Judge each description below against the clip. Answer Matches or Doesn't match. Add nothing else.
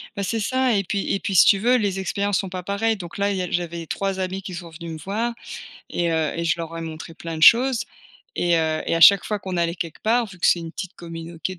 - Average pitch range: Matches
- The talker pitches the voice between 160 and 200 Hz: Matches